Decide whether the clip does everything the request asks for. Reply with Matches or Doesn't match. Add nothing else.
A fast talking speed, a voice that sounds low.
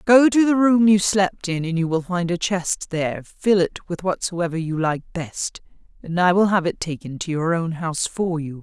Doesn't match